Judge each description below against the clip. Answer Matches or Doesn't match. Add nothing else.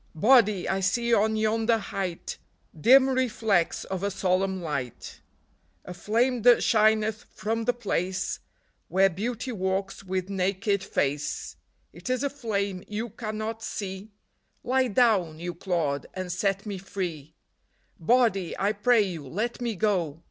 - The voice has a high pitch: Matches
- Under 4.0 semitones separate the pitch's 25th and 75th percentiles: Matches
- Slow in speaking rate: Doesn't match